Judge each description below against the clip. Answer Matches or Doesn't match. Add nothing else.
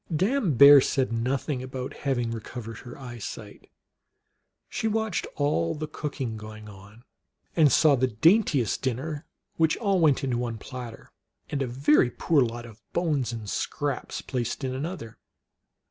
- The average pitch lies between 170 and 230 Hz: Doesn't match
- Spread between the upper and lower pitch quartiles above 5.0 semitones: Doesn't match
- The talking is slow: Doesn't match